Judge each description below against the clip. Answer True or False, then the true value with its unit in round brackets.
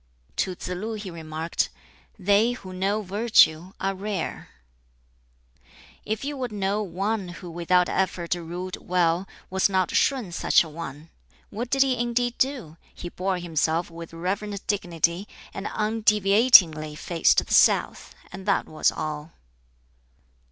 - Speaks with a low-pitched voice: False (185 Hz)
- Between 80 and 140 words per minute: True (135 wpm)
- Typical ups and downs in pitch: True (3.9 semitones)